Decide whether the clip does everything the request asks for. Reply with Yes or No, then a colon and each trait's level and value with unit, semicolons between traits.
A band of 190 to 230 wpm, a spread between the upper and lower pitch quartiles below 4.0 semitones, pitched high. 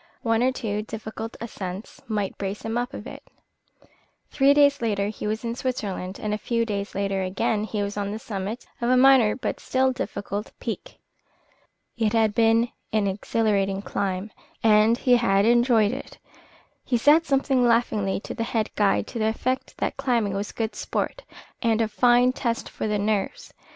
No: average, 175 wpm; average, 2.9 semitones; high, 220 Hz